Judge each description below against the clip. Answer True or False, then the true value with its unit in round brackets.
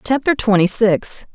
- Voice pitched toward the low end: False (220 Hz)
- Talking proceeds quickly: False (135 wpm)